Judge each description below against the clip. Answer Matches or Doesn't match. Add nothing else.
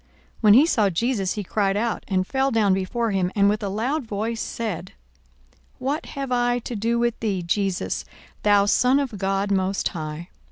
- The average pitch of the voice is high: Matches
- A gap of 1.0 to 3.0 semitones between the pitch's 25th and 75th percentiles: Doesn't match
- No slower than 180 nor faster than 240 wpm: Matches